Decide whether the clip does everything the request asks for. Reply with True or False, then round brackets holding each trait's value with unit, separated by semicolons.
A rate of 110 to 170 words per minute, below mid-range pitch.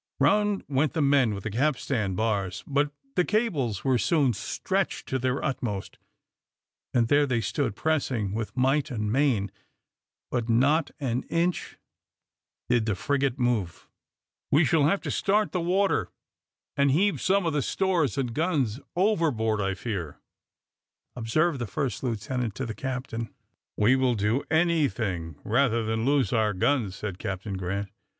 True (150 wpm; 130 Hz)